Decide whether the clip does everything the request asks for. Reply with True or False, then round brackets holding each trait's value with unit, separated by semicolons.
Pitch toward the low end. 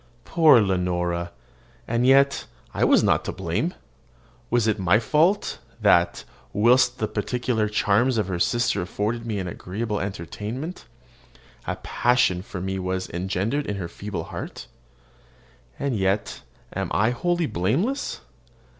True (105 Hz)